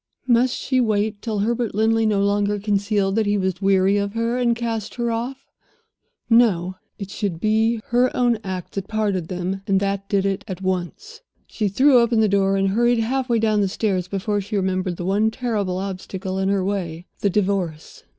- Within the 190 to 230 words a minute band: Yes, average, 195 wpm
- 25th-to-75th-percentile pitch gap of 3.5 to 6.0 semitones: No, average, 2.9 semitones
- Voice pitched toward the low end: No, high, 205 Hz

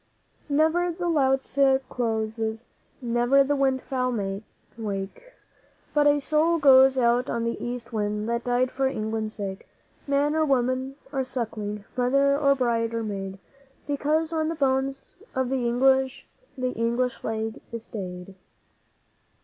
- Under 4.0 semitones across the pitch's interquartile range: Yes, average, 3.5 semitones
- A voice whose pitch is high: Yes, very high, 255 Hz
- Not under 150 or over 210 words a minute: No, average, 140 wpm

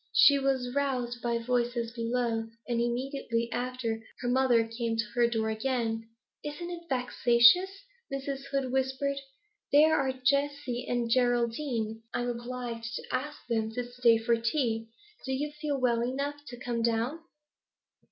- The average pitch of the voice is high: Yes, high, 245 Hz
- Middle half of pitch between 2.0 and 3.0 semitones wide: Yes, average, 2.7 semitones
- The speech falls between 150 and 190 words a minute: No, average, 140 wpm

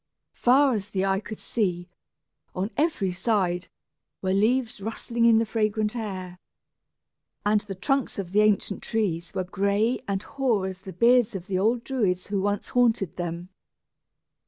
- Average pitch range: Yes, average, 3.4 semitones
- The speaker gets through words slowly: No, average, 160 wpm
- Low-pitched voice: No, high, 205 Hz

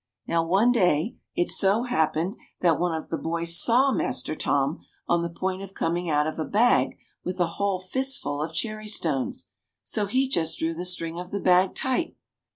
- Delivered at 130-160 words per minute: No, average, 190 wpm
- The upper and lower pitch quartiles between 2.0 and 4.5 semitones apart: Yes, average, 4.2 semitones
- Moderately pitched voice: Yes, medium, 180 Hz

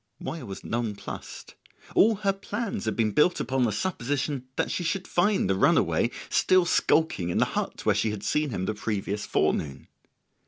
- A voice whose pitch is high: No, low, 130 Hz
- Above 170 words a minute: Yes, average, 180 wpm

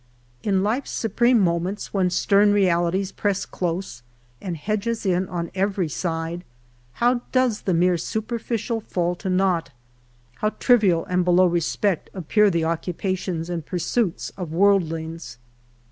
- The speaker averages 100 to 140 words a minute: Yes, slow, 135 wpm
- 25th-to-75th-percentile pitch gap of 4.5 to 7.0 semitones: No, average, 3.3 semitones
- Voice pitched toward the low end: No, medium, 185 Hz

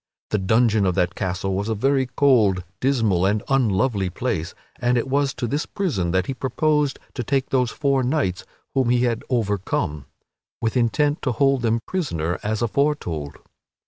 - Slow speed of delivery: No, average, 170 wpm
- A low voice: Yes, low, 120 Hz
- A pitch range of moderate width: No, wide, 5.8 semitones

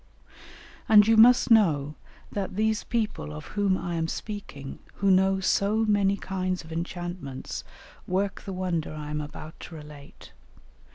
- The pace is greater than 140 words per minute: Yes, average, 150 wpm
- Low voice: No, medium, 185 Hz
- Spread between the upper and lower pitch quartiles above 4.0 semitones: Yes, average, 4.6 semitones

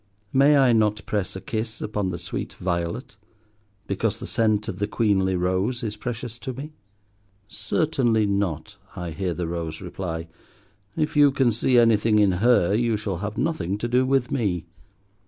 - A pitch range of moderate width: Yes, average, 4.3 semitones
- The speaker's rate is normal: Yes, average, 170 wpm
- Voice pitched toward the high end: No, low, 105 Hz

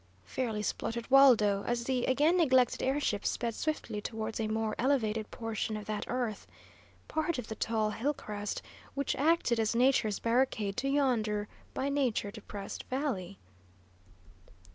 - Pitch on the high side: Yes, high, 230 Hz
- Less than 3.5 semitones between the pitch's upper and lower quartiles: No, average, 3.9 semitones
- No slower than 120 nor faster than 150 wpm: Yes, average, 145 wpm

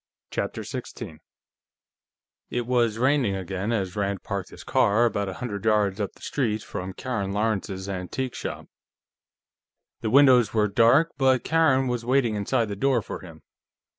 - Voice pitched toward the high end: No, low, 110 Hz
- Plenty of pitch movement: No, average, 4.2 semitones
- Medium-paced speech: Yes, average, 155 wpm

